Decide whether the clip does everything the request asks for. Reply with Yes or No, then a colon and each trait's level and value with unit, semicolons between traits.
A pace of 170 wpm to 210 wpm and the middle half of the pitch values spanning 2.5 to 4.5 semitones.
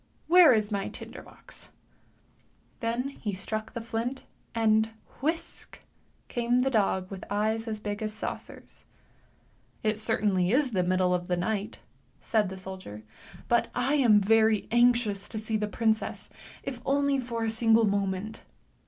No: average, 155 wpm; average, 2.9 semitones